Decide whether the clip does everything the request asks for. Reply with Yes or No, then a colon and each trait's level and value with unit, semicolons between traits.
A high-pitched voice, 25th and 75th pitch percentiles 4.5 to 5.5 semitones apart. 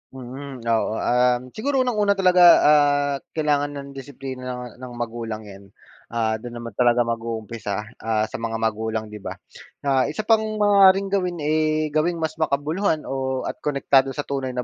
No: low, 135 Hz; average, 5.0 semitones